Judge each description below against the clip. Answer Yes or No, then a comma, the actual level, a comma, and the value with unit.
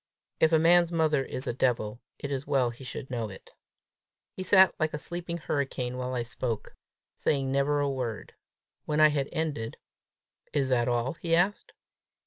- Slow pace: No, average, 175 wpm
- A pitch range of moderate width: Yes, average, 4.0 semitones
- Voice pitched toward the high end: No, medium, 140 Hz